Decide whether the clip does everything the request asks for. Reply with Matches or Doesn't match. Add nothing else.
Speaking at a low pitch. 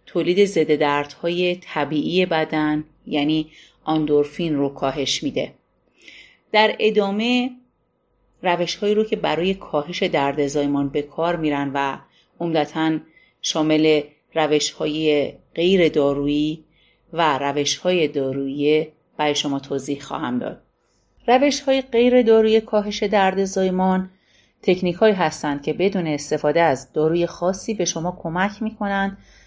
Doesn't match